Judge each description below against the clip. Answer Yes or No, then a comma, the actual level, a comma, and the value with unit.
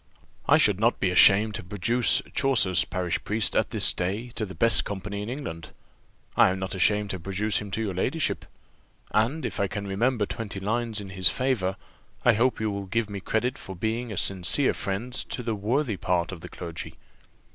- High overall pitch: No, low, 105 Hz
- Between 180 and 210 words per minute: Yes, average, 200 wpm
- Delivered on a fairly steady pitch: No, average, 3.4 semitones